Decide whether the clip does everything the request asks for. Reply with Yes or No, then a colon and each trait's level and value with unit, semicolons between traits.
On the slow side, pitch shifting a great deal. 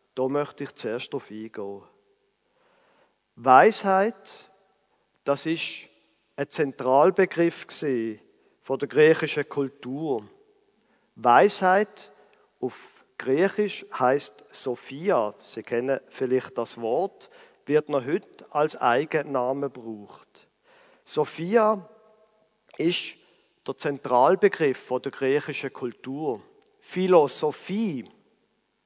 Yes: slow, 85 wpm; wide, 8.0 semitones